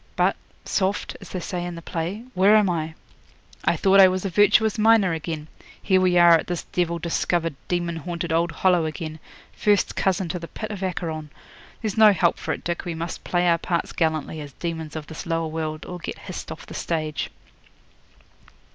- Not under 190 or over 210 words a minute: Yes, average, 200 wpm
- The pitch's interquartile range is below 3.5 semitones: Yes, narrow, 2.5 semitones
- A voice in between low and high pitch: Yes, medium, 175 Hz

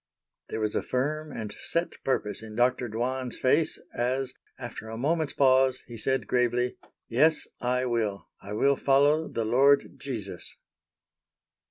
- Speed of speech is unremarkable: Yes, average, 145 wpm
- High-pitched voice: No, low, 125 Hz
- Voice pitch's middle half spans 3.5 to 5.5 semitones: No, average, 3.0 semitones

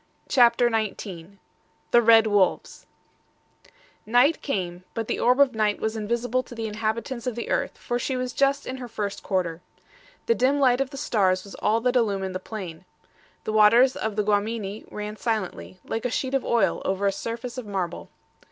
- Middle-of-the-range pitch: No, high, 225 Hz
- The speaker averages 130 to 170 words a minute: No, average, 185 wpm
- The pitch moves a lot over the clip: No, average, 3.4 semitones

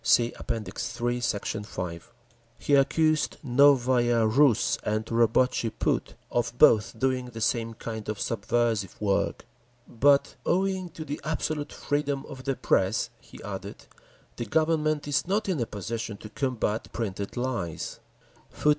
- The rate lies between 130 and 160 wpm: Yes, slow, 135 wpm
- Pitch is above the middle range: No, low, 120 Hz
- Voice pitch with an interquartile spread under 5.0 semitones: Yes, average, 4.5 semitones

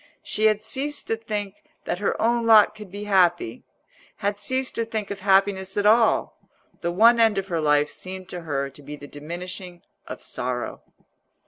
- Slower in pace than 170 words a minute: No, average, 180 wpm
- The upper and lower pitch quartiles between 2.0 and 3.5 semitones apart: No, average, 4.0 semitones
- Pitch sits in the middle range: No, high, 195 Hz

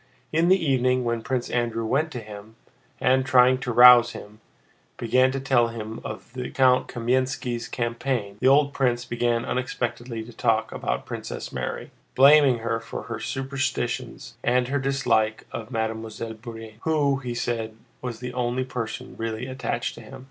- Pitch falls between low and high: No, low, 120 Hz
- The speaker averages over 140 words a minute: Yes, average, 165 wpm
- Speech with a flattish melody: Yes, narrow, 2.2 semitones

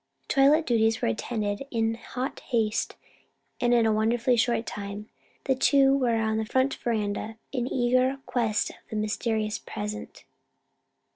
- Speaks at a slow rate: No, average, 150 wpm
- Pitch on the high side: Yes, high, 230 Hz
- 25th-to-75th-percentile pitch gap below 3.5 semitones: Yes, average, 2.9 semitones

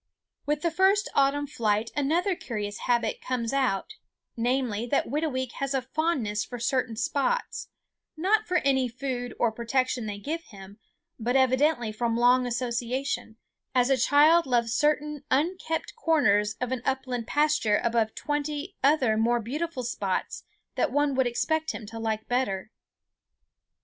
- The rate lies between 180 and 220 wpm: No, average, 145 wpm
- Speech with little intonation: No, average, 4.2 semitones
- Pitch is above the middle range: Yes, very high, 255 Hz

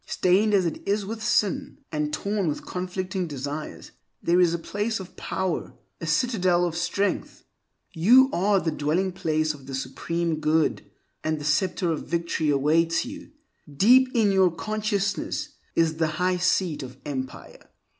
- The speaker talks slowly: No, average, 155 wpm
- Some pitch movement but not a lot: Yes, average, 4.2 semitones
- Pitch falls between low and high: Yes, medium, 175 Hz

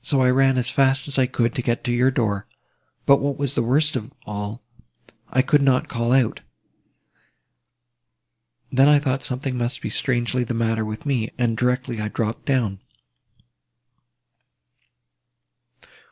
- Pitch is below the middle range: Yes, low, 125 Hz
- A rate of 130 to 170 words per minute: Yes, average, 145 wpm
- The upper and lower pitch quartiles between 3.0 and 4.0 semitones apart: No, narrow, 2.5 semitones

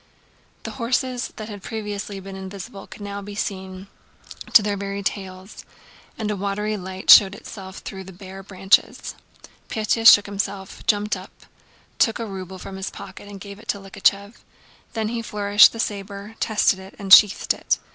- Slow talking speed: No, average, 170 wpm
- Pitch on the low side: No, high, 200 Hz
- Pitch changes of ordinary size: No, narrow, 1.6 semitones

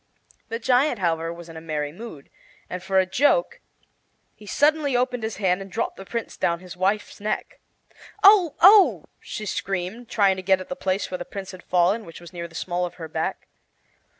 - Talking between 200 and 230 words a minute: Yes, fast, 205 wpm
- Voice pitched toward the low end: No, high, 190 Hz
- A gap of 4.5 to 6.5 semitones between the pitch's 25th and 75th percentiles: Yes, average, 5.0 semitones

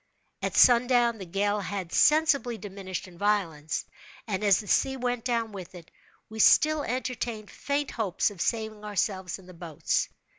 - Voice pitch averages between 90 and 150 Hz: No, high, 210 Hz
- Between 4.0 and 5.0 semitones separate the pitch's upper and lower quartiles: Yes, average, 4.4 semitones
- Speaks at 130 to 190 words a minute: Yes, average, 160 wpm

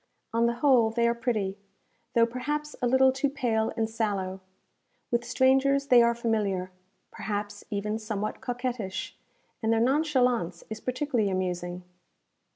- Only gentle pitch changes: No, average, 3.6 semitones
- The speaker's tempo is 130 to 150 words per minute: Yes, average, 140 wpm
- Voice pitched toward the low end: No, high, 230 Hz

